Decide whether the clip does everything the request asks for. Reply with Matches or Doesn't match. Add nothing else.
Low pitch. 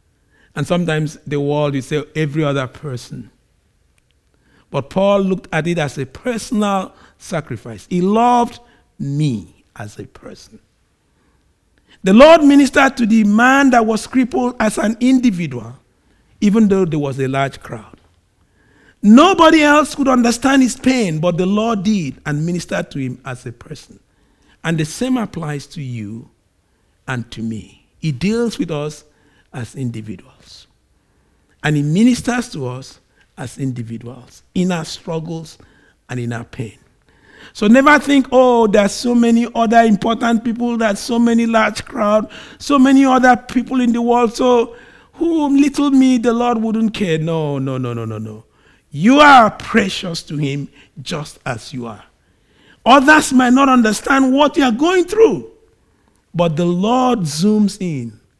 Doesn't match